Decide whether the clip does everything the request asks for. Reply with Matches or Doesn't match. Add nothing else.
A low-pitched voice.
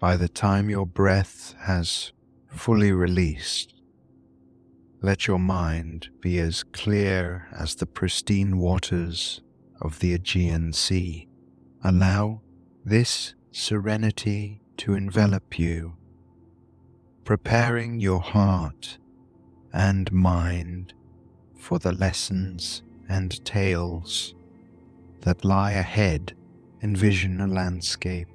Matches